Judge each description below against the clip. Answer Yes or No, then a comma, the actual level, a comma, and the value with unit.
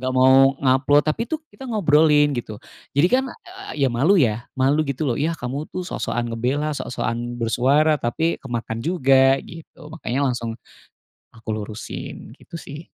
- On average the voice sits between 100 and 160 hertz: Yes, low, 135 Hz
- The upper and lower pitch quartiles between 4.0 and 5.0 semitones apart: Yes, average, 4.3 semitones